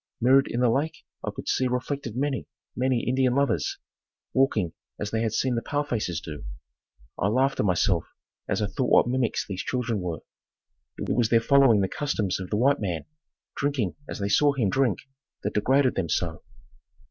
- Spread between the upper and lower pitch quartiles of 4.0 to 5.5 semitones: Yes, average, 4.8 semitones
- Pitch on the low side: Yes, low, 120 Hz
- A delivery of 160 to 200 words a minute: Yes, average, 185 wpm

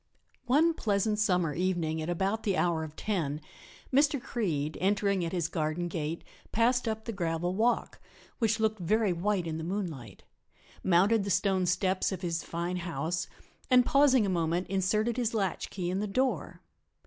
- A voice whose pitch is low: No, high, 190 Hz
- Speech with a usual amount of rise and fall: Yes, average, 4.3 semitones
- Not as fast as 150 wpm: No, average, 165 wpm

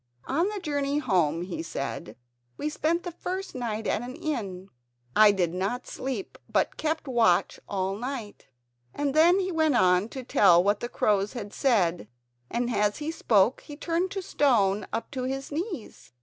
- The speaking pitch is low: No, high, 245 Hz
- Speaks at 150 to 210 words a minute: Yes, average, 175 wpm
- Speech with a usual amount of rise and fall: No, wide, 7.2 semitones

